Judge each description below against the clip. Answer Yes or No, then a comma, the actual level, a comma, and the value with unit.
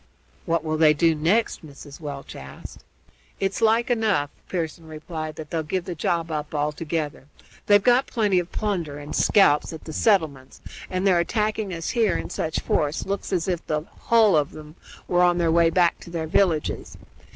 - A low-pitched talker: No, medium, 165 Hz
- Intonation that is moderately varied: Yes, average, 3.9 semitones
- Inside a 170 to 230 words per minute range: Yes, average, 185 wpm